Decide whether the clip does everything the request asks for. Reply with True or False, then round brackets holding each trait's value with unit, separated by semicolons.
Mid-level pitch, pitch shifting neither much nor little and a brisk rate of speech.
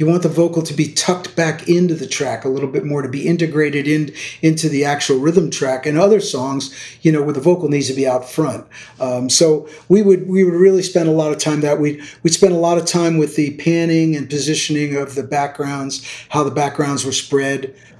True (150 Hz; 3.1 semitones; 235 wpm)